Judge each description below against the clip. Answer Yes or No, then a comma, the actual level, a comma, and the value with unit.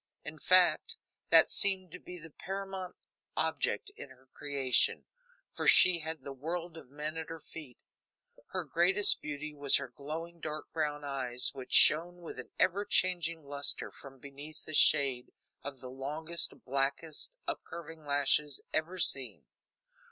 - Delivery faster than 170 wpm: No, average, 150 wpm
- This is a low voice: No, medium, 155 Hz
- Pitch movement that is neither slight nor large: Yes, average, 3.5 semitones